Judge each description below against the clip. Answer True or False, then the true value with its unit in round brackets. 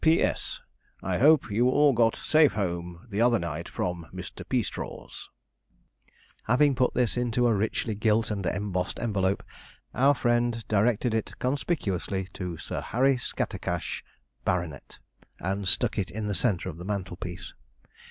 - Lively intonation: False (4.8 semitones)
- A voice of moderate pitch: False (105 Hz)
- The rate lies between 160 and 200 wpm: False (140 wpm)